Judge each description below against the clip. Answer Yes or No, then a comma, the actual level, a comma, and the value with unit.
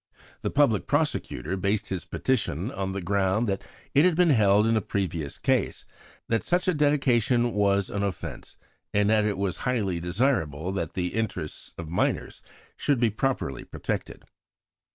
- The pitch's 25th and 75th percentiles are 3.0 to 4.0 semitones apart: No, average, 4.8 semitones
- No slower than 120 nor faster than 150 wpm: No, average, 160 wpm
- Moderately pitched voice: No, low, 105 Hz